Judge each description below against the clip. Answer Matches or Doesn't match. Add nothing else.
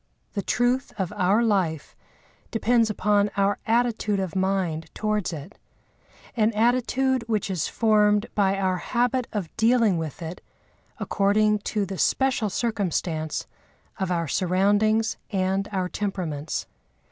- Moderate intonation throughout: Matches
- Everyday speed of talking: Doesn't match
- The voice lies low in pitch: Doesn't match